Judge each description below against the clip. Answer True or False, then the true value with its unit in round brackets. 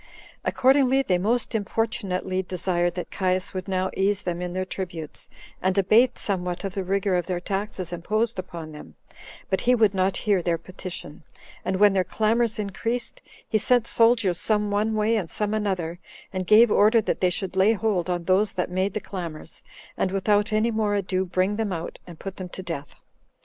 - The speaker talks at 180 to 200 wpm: True (190 wpm)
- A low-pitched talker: False (195 Hz)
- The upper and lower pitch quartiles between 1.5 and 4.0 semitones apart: True (2.9 semitones)